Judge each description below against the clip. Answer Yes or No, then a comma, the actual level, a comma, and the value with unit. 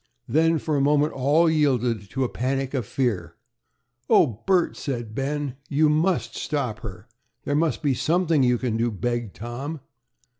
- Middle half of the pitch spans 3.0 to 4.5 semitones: Yes, average, 4.1 semitones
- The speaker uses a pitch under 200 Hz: Yes, low, 135 Hz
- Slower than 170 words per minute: Yes, average, 160 wpm